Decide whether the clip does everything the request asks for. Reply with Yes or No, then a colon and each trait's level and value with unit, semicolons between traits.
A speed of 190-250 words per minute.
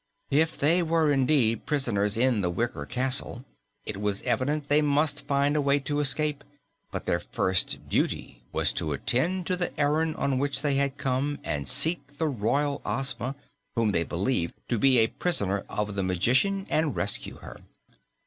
No: average, 170 wpm